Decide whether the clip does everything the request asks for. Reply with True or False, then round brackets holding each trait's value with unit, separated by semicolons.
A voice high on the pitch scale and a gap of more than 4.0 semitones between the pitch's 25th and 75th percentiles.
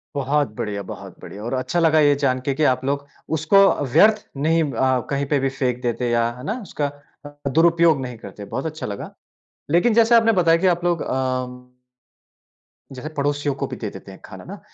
False (140 Hz; 4.5 semitones)